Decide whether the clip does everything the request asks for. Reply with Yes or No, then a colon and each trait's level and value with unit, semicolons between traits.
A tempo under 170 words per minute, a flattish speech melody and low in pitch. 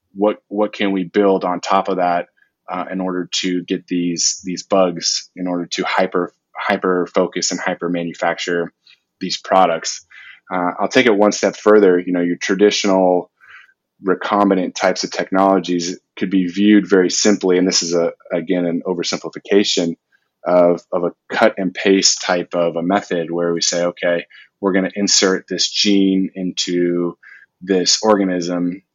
Yes: average, 160 wpm; narrow, 1.8 semitones; very low, 90 Hz